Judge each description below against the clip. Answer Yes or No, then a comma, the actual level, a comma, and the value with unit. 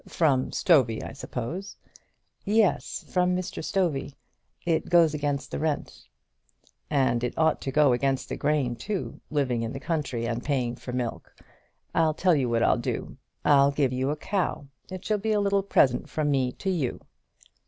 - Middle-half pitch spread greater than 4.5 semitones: Yes, average, 5.1 semitones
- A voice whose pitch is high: No, medium, 145 Hz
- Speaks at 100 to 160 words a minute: No, average, 175 wpm